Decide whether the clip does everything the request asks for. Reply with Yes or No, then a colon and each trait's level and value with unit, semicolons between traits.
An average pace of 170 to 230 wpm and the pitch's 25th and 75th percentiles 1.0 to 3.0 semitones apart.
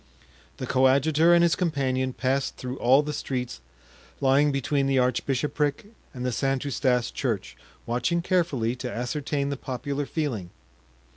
No: average, 140 wpm; narrow, 2.6 semitones